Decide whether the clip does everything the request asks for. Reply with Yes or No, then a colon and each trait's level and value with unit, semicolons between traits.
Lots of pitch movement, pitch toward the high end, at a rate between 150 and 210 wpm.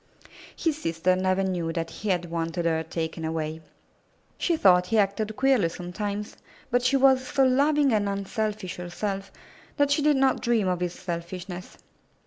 Yes: wide, 6.0 semitones; high, 195 Hz; average, 160 wpm